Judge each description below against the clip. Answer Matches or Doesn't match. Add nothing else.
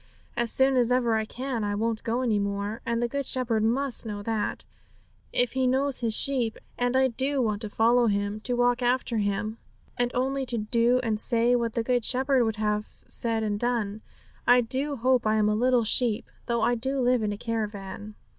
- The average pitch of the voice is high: Matches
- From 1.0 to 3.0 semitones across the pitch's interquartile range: Matches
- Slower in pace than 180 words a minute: Doesn't match